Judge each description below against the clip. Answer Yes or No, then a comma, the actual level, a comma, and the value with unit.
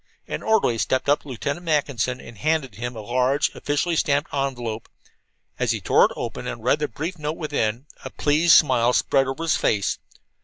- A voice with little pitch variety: No, average, 3.9 semitones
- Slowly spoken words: No, average, 190 wpm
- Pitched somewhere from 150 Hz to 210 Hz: No, medium, 140 Hz